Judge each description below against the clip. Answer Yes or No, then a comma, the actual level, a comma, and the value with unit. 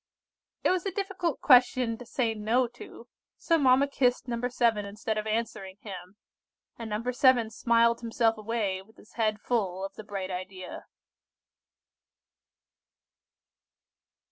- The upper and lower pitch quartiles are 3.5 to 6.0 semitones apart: No, average, 3.1 semitones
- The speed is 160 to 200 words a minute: No, slow, 135 wpm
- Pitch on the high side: Yes, high, 230 Hz